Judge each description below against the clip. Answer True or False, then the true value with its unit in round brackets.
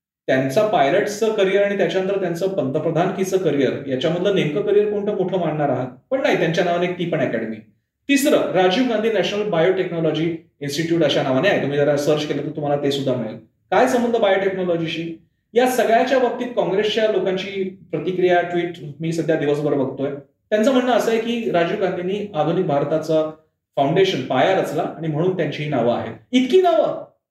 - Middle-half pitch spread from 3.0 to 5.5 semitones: True (5.1 semitones)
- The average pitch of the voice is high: False (175 Hz)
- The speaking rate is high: True (165 wpm)